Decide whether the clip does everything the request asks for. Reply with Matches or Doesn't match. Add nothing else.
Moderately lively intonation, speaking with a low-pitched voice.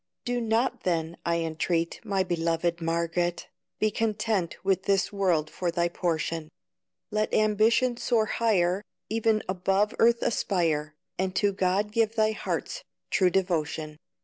Doesn't match